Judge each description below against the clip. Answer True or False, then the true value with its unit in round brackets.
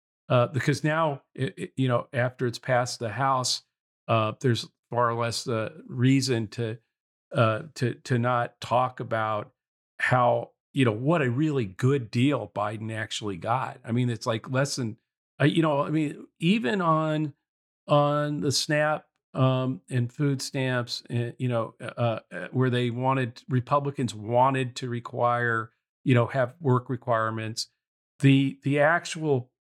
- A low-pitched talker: True (125 Hz)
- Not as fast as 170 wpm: True (155 wpm)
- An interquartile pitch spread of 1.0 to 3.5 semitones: True (3.1 semitones)